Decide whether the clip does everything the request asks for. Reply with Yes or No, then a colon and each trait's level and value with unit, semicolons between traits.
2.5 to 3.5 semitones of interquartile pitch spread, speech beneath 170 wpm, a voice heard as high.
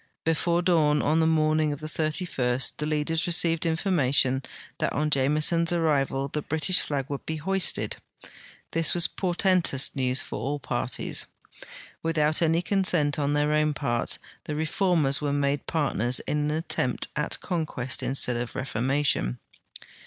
No: average, 2.9 semitones; average, 145 wpm; medium, 150 Hz